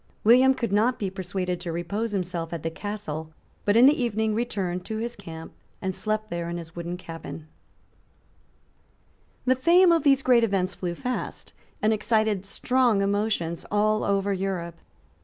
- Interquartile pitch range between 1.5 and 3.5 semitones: No, average, 4.6 semitones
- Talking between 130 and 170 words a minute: Yes, average, 160 wpm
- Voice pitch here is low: No, high, 200 Hz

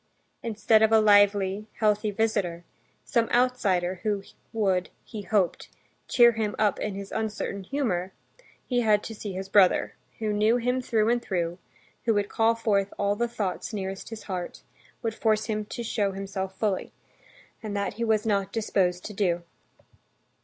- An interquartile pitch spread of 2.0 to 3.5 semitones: Yes, narrow, 2.4 semitones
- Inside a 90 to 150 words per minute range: No, average, 165 wpm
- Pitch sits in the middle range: No, high, 210 Hz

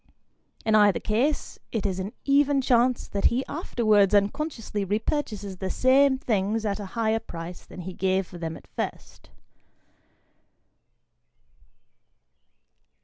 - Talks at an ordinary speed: No, slow, 125 wpm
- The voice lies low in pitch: No, high, 215 Hz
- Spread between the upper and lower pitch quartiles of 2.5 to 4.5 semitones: No, average, 4.9 semitones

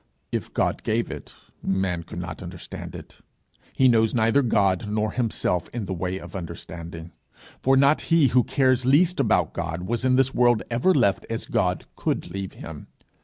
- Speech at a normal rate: Yes, average, 180 wpm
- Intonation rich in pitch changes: Yes, wide, 6.1 semitones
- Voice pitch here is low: Yes, low, 110 Hz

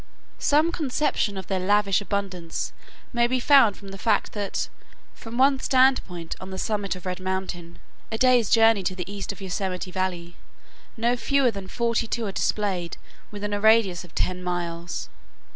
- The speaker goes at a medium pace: Yes, average, 170 wpm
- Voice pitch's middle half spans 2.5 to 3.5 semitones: No, average, 4.0 semitones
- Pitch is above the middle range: Yes, high, 200 Hz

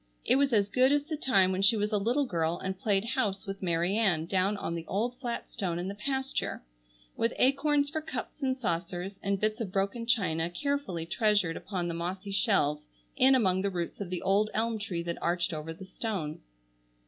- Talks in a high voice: Yes, high, 200 Hz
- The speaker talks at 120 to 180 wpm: No, fast, 205 wpm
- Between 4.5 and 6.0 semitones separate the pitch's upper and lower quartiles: Yes, average, 5.0 semitones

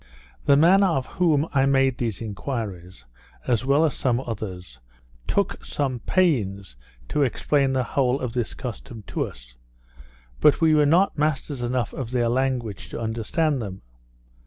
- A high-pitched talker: No, low, 130 Hz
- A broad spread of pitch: No, average, 4.3 semitones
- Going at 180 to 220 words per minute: No, average, 155 wpm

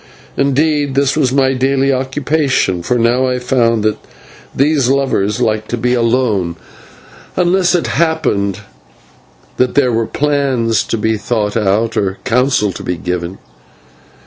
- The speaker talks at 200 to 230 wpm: No, average, 140 wpm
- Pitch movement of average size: Yes, average, 4.2 semitones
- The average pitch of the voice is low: Yes, low, 125 Hz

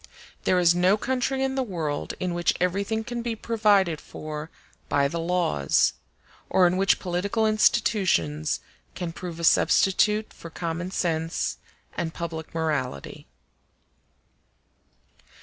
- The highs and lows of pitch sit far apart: No, average, 4.4 semitones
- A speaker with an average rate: No, slow, 125 wpm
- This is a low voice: No, medium, 180 Hz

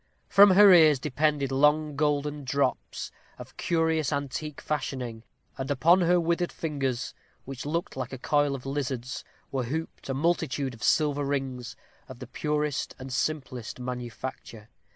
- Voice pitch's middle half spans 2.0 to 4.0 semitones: Yes, average, 2.9 semitones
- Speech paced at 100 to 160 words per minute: Yes, average, 145 wpm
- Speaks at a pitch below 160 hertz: Yes, medium, 140 Hz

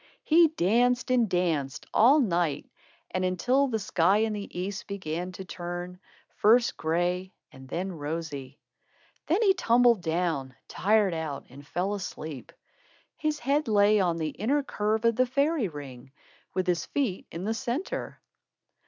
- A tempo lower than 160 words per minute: Yes, average, 150 wpm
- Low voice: No, high, 190 Hz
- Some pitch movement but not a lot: No, wide, 6.2 semitones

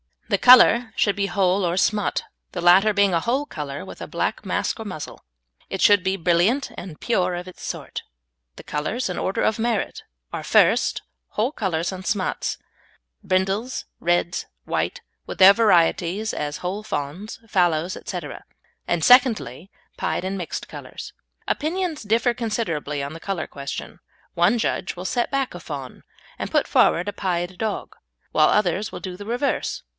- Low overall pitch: No, high, 190 Hz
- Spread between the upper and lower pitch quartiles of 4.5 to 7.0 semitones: No, average, 4.1 semitones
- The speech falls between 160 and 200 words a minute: Yes, average, 170 wpm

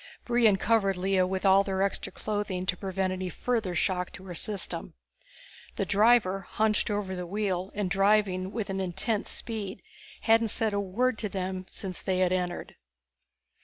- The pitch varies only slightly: Yes, narrow, 2.3 semitones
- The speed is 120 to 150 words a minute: No, average, 165 wpm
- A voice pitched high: Yes, high, 195 Hz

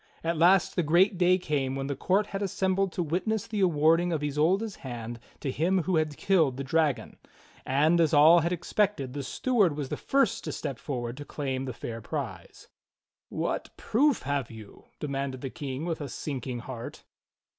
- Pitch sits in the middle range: Yes, medium, 155 Hz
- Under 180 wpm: No, average, 185 wpm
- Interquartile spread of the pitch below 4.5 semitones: No, average, 5.2 semitones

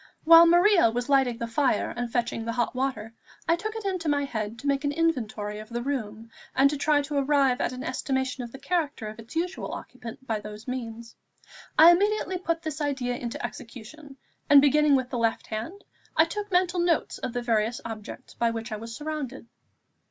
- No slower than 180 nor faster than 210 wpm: Yes, average, 200 wpm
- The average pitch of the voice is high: Yes, very high, 265 Hz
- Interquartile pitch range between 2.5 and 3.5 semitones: No, average, 5.1 semitones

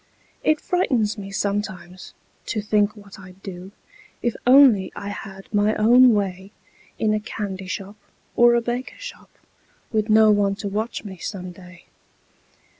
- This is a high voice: Yes, high, 205 Hz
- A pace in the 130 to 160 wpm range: Yes, average, 150 wpm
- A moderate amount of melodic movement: No, narrow, 2.3 semitones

